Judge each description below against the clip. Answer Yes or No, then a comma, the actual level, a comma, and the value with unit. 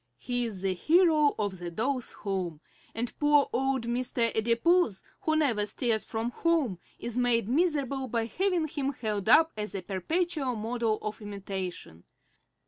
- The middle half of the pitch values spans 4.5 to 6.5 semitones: Yes, wide, 5.6 semitones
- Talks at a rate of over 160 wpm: No, average, 150 wpm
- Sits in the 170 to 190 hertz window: No, high, 235 Hz